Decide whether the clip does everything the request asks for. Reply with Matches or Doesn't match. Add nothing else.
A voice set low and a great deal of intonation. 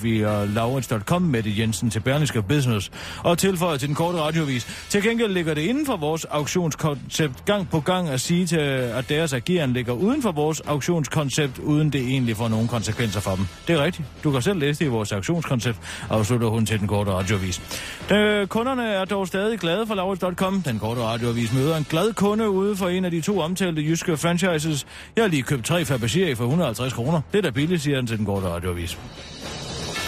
Doesn't match